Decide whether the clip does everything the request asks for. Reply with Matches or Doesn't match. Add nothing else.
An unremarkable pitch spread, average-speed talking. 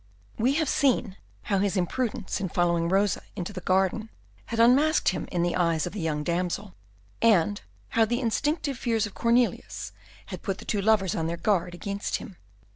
Matches